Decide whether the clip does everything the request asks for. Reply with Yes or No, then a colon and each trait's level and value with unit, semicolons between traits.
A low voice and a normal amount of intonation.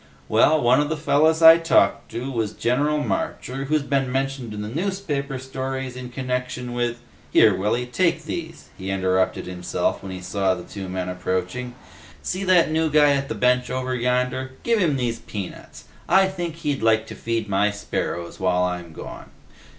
No: low, 125 Hz; wide, 6.0 semitones